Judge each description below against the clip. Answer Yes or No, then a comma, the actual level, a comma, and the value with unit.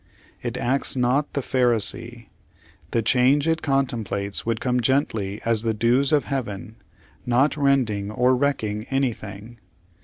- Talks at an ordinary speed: No, slow, 130 wpm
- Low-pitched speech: Yes, low, 120 Hz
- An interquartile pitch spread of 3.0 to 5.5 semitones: Yes, average, 3.5 semitones